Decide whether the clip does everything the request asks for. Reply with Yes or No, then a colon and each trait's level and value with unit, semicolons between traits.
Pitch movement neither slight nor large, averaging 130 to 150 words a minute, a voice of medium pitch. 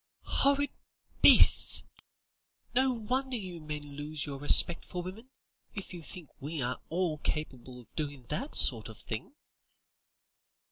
No: wide, 7.3 semitones; slow, 135 wpm; medium, 165 Hz